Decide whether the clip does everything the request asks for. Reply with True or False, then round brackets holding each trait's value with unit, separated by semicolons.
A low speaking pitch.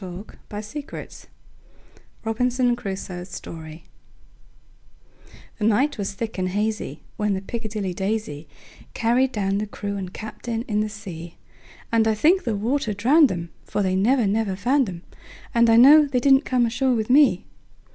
False (215 Hz)